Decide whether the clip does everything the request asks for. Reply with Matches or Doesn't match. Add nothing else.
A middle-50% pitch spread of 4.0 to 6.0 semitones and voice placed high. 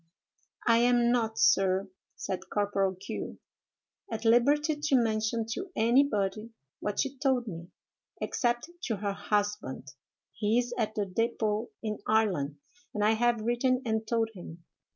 Doesn't match